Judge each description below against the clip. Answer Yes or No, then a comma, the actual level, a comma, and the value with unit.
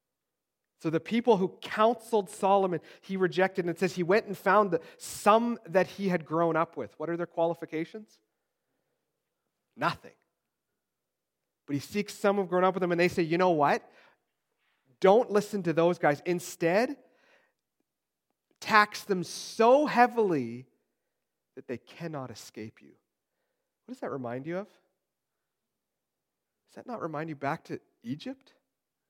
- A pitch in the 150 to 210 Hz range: Yes, medium, 185 Hz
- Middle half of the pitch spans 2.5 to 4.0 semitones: No, average, 4.4 semitones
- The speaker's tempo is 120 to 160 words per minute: Yes, average, 150 wpm